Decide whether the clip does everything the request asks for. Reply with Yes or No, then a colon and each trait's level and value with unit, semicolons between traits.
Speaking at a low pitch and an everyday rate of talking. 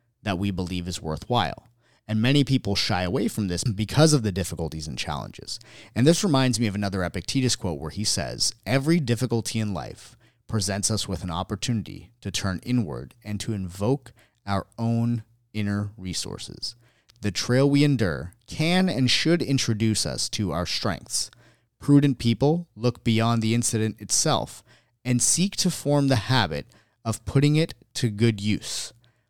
Yes: low, 115 Hz; average, 160 wpm